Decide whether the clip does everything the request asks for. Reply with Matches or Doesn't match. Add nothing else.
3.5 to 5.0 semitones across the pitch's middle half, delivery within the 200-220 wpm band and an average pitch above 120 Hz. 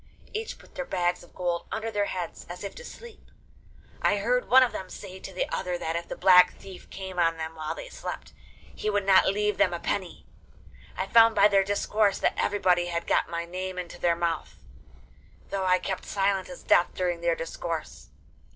Doesn't match